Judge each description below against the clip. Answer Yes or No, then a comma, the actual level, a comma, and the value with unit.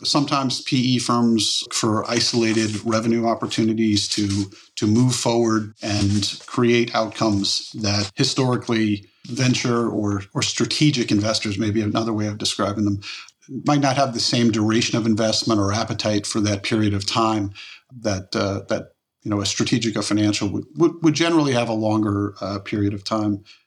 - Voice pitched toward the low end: Yes, low, 110 Hz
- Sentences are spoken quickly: No, average, 155 wpm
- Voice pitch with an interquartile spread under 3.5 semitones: Yes, narrow, 2.4 semitones